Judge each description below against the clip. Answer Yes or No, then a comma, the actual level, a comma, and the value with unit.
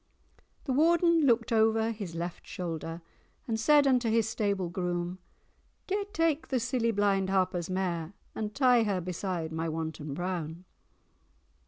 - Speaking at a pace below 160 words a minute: Yes, average, 140 wpm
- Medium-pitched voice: No, high, 200 Hz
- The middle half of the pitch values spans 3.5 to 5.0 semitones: No, wide, 5.5 semitones